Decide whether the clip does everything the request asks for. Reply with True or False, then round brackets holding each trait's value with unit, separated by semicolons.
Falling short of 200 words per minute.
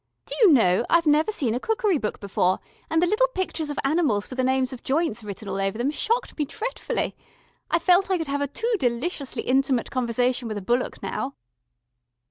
False (205 wpm)